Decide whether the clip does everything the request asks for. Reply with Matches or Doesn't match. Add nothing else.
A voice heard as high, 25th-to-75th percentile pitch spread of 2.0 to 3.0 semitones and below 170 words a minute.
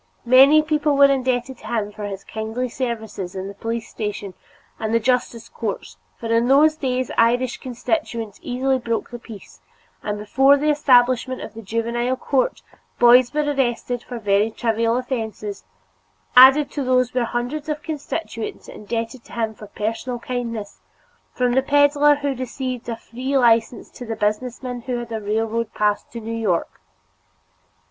Matches